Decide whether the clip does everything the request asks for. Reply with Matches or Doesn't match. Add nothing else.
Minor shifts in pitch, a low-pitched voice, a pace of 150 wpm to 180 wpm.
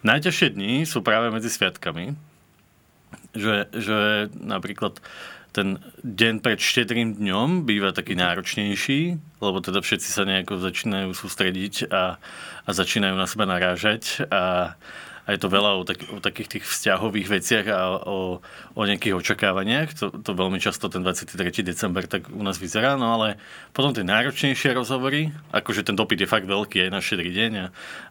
Doesn't match